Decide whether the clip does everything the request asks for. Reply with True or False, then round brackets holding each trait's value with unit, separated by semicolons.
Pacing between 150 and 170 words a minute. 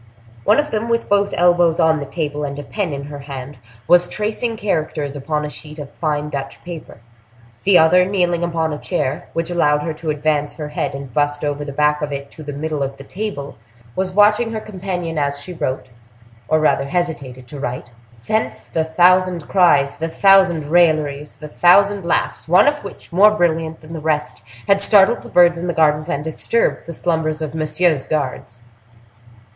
False (195 wpm)